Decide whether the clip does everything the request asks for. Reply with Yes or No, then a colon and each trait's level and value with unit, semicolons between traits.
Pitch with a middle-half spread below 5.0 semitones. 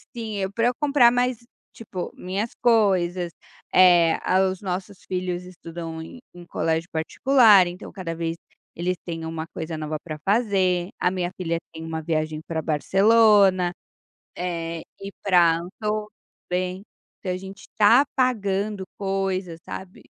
Yes: average, 3.4 semitones